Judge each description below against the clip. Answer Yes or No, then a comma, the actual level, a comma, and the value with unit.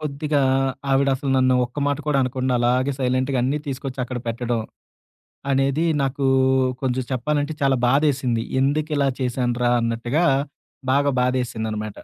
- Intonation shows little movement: Yes, narrow, 2.3 semitones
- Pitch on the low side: Yes, low, 130 Hz